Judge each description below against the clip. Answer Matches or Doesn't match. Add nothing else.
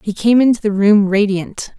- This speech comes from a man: Doesn't match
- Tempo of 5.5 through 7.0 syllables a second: Doesn't match